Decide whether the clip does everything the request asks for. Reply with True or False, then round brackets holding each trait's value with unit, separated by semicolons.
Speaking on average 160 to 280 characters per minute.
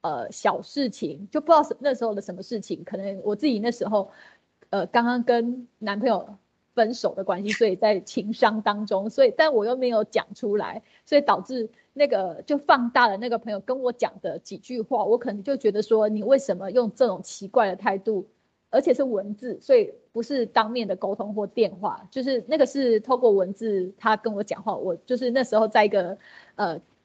False (300 characters per minute)